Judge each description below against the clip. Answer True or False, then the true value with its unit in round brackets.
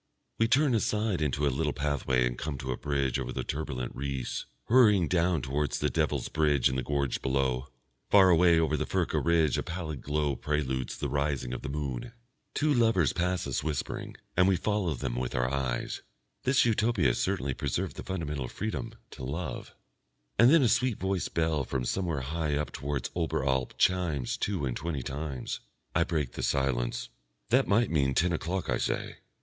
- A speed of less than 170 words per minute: False (185 wpm)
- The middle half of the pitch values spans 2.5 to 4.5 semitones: False (5.4 semitones)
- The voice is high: False (75 Hz)